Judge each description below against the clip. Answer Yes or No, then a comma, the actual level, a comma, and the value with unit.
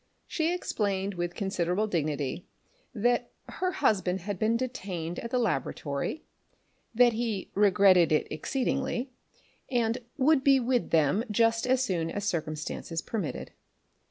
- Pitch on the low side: No, high, 210 Hz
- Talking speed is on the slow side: Yes, slow, 130 wpm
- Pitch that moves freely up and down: Yes, wide, 6.0 semitones